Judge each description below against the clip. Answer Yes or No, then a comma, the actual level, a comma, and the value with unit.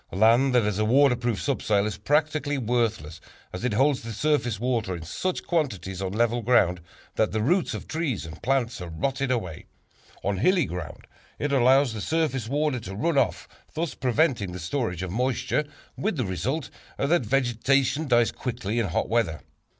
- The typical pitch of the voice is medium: No, low, 120 Hz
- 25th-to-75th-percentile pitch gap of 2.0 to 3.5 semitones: No, average, 5.2 semitones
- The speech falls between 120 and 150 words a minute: No, average, 175 wpm